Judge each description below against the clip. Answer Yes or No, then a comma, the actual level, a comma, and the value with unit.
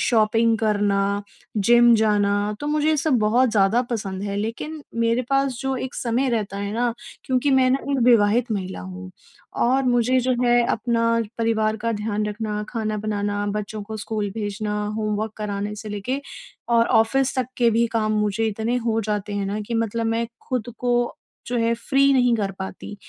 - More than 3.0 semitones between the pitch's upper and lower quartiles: No, average, 2.7 semitones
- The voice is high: Yes, high, 225 Hz